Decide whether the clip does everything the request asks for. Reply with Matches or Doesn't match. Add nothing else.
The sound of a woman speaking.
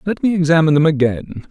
Doesn't match